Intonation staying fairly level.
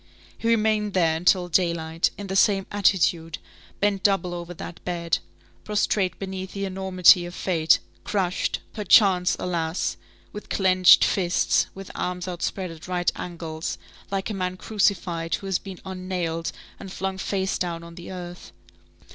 Yes: narrow, 2.0 semitones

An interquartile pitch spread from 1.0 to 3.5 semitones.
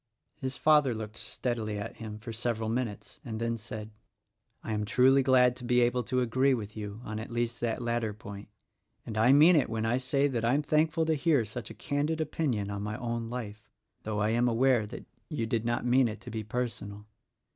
Yes: average, 3.0 semitones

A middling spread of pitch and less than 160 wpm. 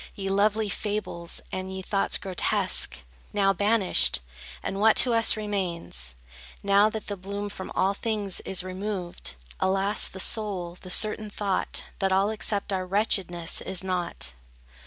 No: narrow, 2.0 semitones; average, 145 wpm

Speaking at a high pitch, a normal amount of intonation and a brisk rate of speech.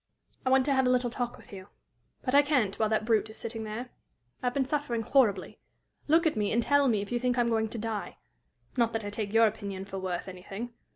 Yes: high, 230 Hz; average, 3.3 semitones; fast, 250 wpm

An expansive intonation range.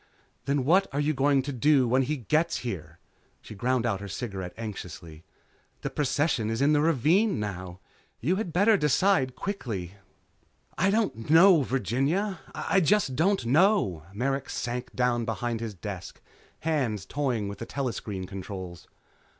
Yes: wide, 6.7 semitones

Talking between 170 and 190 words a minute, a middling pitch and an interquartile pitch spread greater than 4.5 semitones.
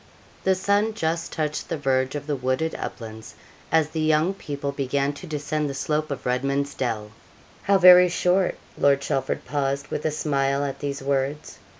No: average, 175 wpm; medium, 145 Hz; average, 2.7 semitones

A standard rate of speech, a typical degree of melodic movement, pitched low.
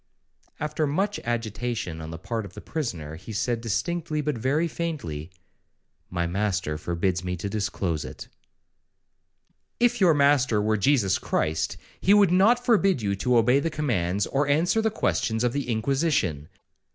No: average, 155 wpm; wide, 8.6 semitones; low, 120 Hz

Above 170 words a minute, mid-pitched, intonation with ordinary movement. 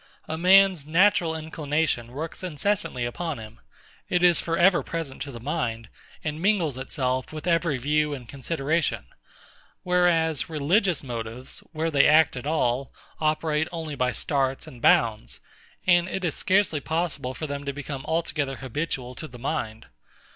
No: average, 155 wpm; medium, 150 Hz; average, 4.1 semitones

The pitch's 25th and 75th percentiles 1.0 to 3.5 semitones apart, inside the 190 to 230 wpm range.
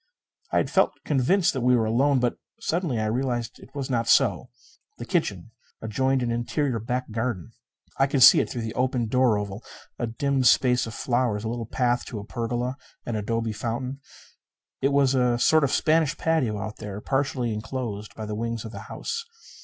Yes: average, 2.9 semitones; average, 195 wpm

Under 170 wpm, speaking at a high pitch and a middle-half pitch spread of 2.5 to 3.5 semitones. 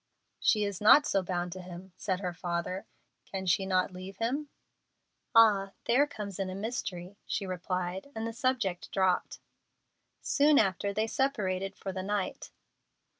Yes: average, 155 wpm; high, 195 Hz; average, 3.2 semitones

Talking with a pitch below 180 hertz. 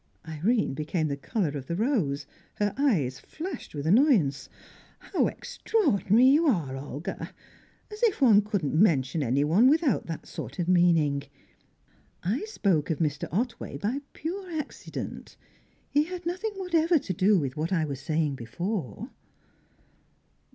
No: medium, 185 Hz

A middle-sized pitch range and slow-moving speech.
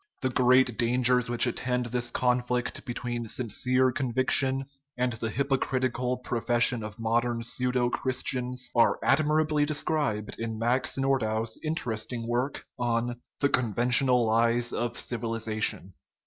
No: narrow, 1.7 semitones; slow, 125 wpm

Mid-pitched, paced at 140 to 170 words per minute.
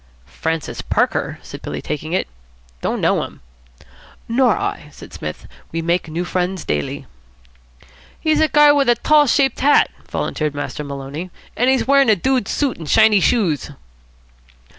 No: high, 195 Hz; average, 155 wpm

